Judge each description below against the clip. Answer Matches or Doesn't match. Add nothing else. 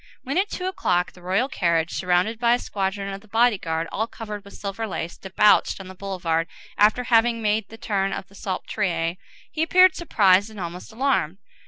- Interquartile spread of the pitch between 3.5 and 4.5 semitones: Matches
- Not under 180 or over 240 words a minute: Matches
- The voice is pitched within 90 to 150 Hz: Doesn't match